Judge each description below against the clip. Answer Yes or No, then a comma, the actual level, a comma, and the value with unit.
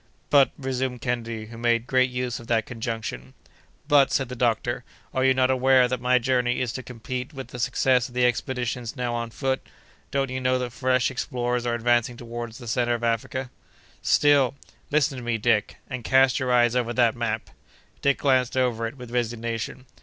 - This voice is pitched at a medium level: No, low, 125 Hz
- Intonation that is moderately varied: No, narrow, 1.7 semitones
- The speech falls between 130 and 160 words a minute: No, average, 190 wpm